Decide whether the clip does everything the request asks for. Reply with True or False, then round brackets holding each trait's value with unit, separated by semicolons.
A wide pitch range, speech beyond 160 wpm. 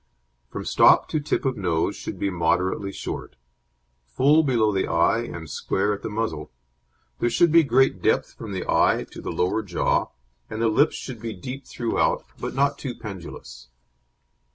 True (6.2 semitones; 175 wpm)